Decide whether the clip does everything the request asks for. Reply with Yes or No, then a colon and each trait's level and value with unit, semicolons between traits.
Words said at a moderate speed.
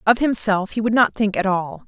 No: fast, 255 wpm